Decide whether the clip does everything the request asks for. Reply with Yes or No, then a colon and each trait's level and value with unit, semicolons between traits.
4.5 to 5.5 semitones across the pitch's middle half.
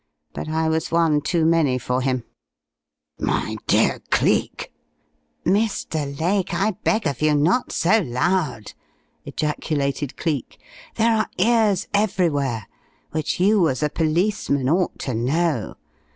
Yes: average, 5.1 semitones